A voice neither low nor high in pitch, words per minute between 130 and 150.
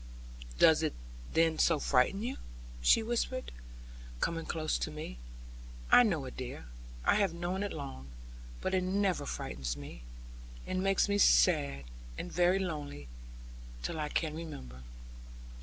Yes: medium, 160 Hz; average, 140 wpm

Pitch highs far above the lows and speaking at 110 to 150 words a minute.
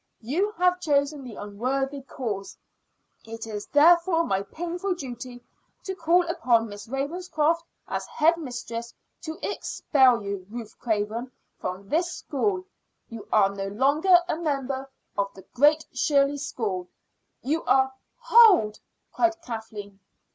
Yes: wide, 6.8 semitones; slow, 135 wpm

